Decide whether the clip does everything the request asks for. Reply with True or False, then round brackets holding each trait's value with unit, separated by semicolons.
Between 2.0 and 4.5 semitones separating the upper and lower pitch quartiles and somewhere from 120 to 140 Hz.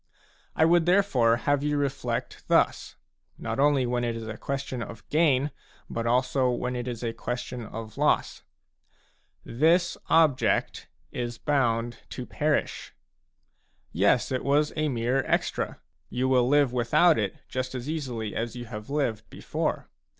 True (3.5 semitones; 125 Hz)